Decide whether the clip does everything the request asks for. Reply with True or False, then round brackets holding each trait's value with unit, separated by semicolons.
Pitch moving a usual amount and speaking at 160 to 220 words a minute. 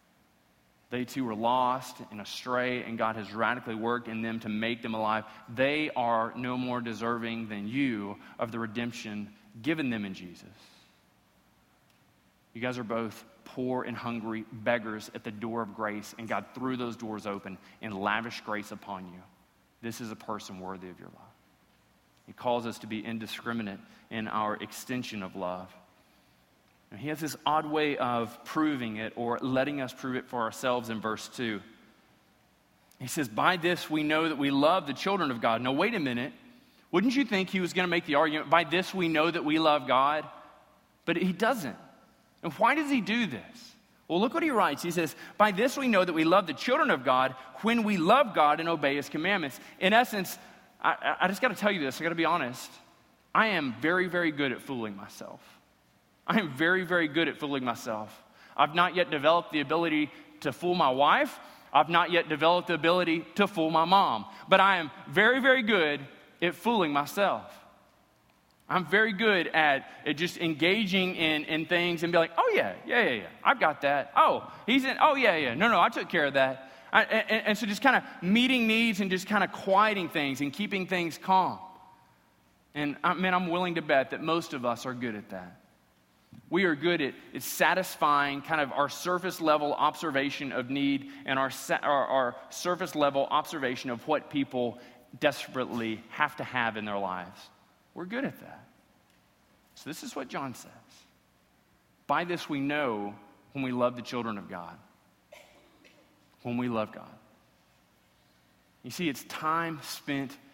False (7.0 semitones; 190 wpm)